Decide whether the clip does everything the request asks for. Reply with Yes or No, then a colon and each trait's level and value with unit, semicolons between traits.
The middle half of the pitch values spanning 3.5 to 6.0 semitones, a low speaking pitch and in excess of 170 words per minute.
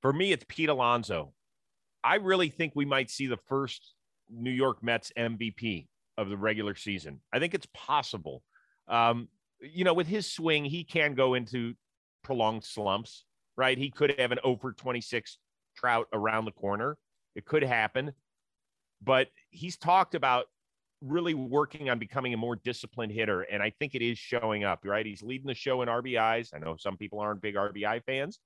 Yes: average, 3.9 semitones; low, 120 Hz; average, 180 wpm